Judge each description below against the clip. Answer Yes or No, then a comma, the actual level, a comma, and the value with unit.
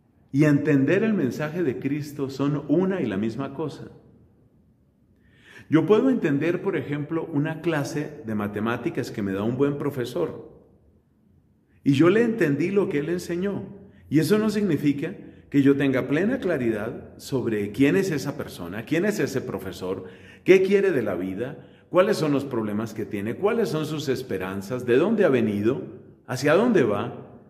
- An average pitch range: No, wide, 6.4 semitones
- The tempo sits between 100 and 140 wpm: No, average, 165 wpm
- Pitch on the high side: No, medium, 145 Hz